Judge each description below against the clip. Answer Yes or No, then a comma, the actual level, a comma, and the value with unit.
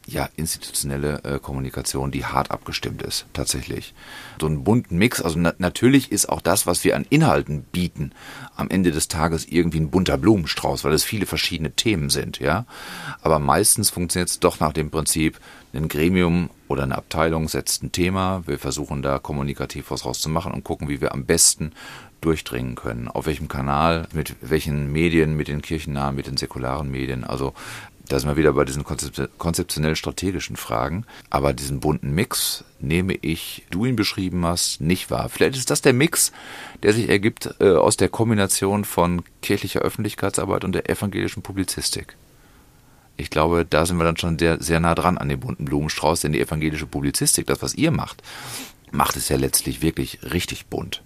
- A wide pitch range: No, average, 3.6 semitones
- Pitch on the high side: No, very low, 80 Hz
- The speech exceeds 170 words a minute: Yes, average, 180 wpm